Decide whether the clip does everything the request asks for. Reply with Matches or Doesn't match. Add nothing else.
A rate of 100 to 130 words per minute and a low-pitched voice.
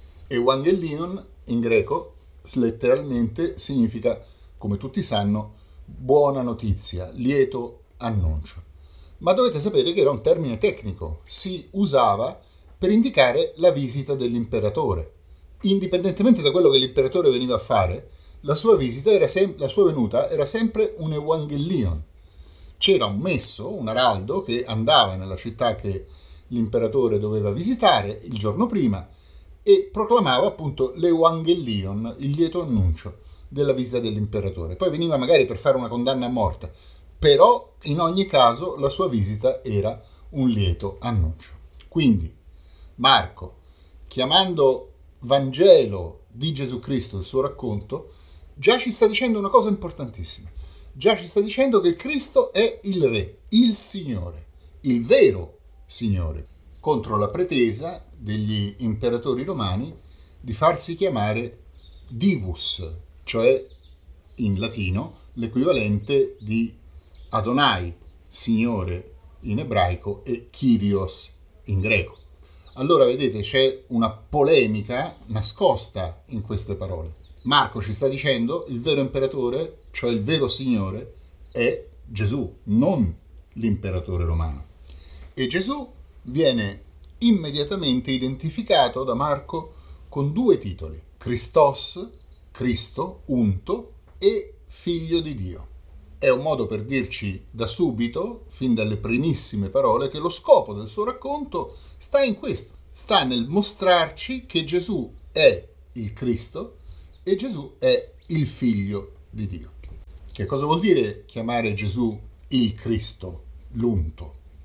Matches